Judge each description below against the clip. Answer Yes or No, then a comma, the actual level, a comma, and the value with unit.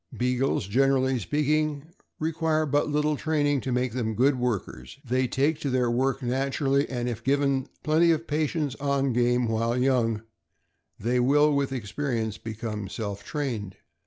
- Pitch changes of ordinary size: Yes, average, 3.3 semitones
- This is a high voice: No, low, 130 Hz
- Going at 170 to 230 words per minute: No, average, 155 wpm